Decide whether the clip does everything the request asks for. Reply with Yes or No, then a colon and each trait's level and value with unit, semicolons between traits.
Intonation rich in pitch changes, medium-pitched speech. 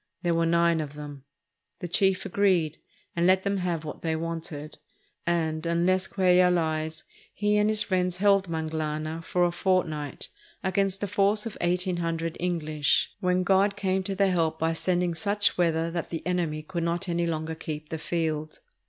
No: average, 2.7 semitones; medium, 170 Hz